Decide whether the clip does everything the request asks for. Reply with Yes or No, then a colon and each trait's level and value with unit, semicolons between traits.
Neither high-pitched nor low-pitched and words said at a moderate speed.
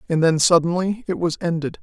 Yes: medium, 170 Hz; average, 195 wpm